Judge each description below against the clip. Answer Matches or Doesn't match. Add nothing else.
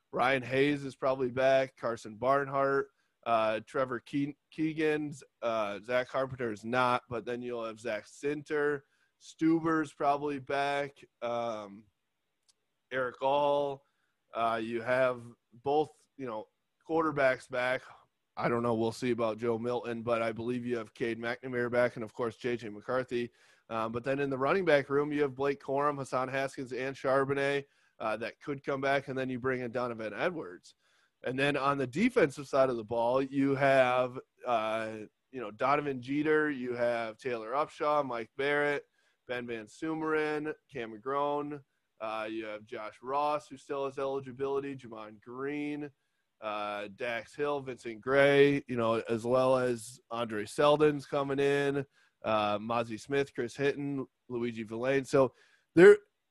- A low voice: Matches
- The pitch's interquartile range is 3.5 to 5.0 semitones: Doesn't match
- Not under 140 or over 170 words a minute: Matches